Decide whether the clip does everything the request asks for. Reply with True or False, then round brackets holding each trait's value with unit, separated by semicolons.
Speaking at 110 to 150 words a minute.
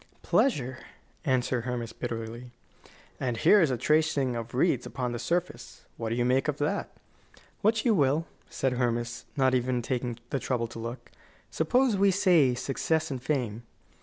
False (165 wpm)